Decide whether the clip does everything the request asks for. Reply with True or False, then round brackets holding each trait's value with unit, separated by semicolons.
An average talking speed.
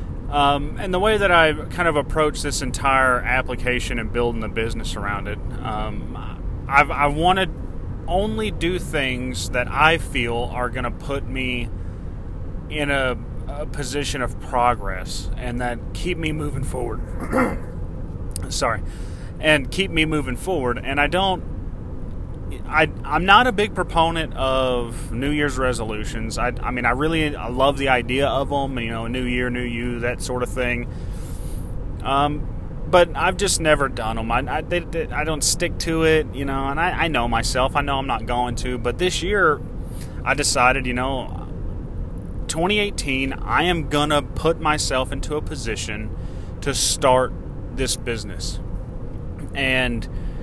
True (160 wpm)